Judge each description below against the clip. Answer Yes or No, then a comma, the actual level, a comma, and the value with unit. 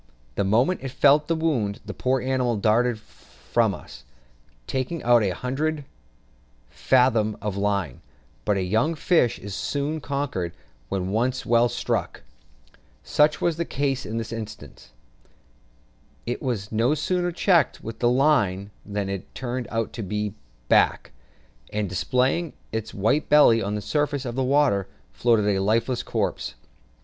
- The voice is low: Yes, low, 120 Hz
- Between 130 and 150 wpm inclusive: Yes, average, 145 wpm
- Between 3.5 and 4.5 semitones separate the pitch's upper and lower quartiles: No, average, 5.2 semitones